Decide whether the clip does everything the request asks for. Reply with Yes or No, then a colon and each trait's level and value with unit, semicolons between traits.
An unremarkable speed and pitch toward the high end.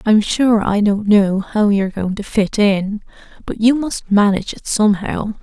Yes: average, 190 wpm; high, 210 Hz